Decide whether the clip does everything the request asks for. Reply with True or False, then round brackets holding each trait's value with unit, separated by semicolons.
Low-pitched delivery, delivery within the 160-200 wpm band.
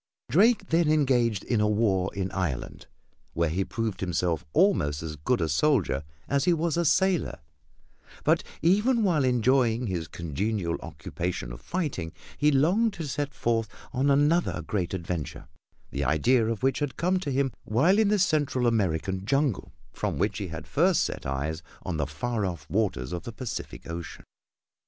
True (115 Hz; 170 wpm)